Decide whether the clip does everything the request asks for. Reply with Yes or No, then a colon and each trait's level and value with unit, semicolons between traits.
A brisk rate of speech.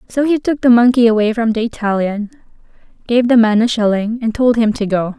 Yes: fast, 220 wpm